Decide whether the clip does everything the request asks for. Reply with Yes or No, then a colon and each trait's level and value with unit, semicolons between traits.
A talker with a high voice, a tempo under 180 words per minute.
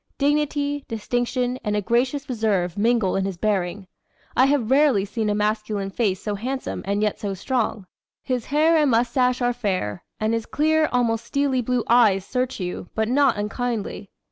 Yes: high, 235 Hz; average, 170 wpm